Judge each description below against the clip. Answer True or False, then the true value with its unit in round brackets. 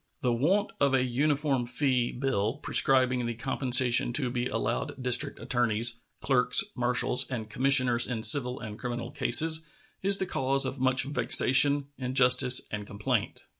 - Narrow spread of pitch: True (2.1 semitones)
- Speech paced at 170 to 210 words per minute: False (145 wpm)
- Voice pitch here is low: True (125 Hz)